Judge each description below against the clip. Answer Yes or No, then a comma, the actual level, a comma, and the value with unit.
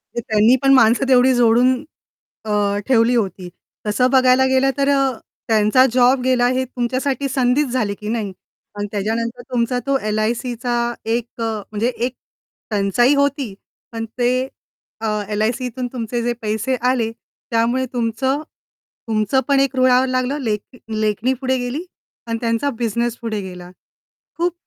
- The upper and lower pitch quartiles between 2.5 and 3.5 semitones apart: Yes, average, 2.8 semitones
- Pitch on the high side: Yes, high, 245 Hz